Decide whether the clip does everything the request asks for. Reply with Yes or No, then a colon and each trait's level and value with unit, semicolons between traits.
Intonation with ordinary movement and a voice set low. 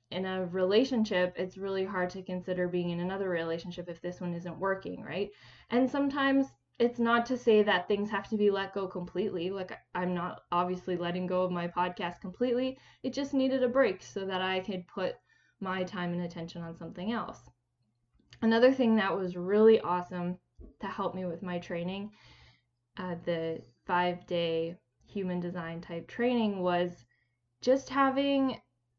No: average, 3.2 semitones; medium, 185 Hz